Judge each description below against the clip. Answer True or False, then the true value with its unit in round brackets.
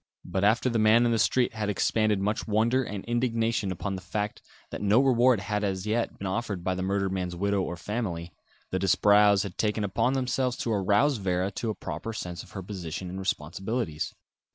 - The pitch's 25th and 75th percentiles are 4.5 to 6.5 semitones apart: False (3.3 semitones)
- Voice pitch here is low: True (105 Hz)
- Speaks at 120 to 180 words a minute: False (200 wpm)